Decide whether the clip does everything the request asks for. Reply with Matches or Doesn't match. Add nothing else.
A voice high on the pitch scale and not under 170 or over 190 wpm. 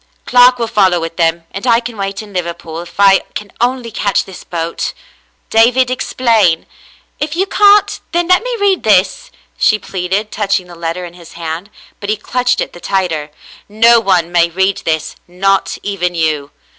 Matches